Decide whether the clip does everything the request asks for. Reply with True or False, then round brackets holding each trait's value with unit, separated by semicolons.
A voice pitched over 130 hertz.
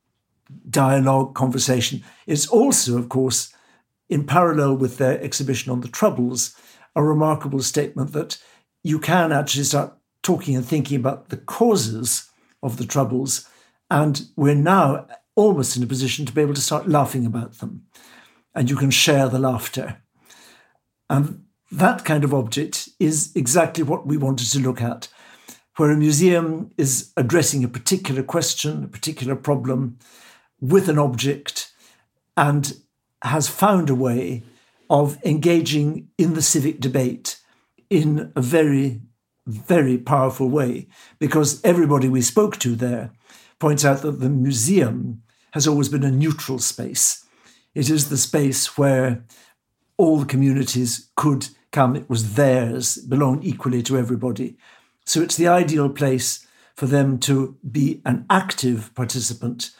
True (140 Hz)